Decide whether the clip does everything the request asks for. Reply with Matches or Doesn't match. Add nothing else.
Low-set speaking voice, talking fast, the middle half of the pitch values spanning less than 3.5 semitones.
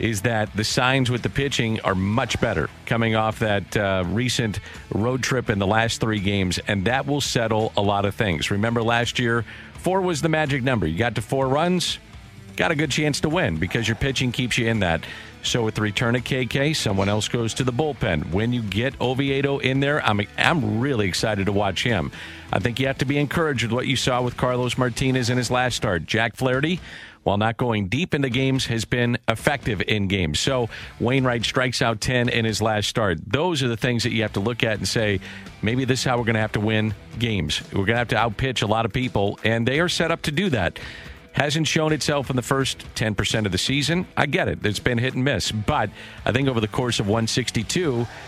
Doesn't match